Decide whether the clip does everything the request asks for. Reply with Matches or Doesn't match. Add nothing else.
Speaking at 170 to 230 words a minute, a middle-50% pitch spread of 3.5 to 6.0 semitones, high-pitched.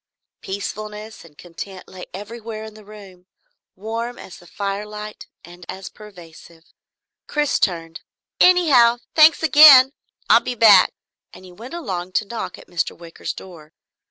Doesn't match